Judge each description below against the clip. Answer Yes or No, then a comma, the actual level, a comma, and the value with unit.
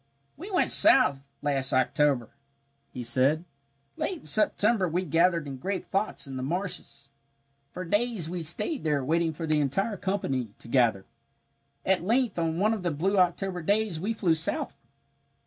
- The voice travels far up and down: Yes, wide, 5.8 semitones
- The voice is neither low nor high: Yes, medium, 170 Hz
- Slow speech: No, average, 165 wpm